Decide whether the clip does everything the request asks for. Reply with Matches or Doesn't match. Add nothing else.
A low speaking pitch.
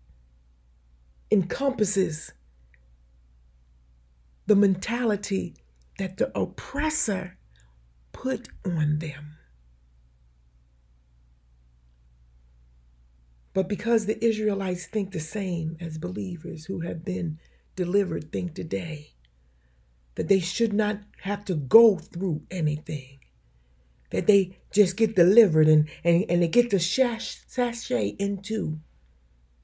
Doesn't match